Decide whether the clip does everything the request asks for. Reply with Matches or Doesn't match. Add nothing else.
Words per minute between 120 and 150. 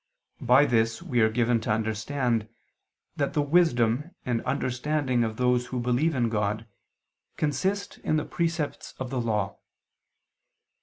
Matches